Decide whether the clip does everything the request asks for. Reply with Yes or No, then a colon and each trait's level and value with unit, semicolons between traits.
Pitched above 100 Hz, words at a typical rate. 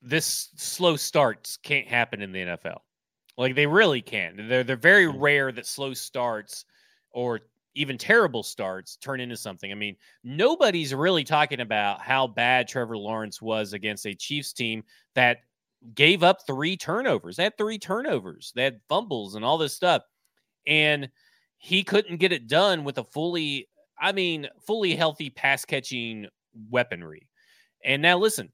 Yes: low, 135 Hz; average, 160 wpm